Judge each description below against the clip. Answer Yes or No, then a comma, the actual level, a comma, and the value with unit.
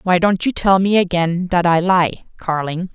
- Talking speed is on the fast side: No, average, 185 wpm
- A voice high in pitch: No, medium, 180 Hz